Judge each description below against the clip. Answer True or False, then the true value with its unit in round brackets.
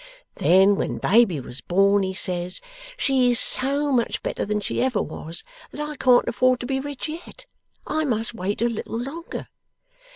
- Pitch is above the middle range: True (240 Hz)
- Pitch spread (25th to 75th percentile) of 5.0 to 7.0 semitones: True (5.5 semitones)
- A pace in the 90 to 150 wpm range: False (175 wpm)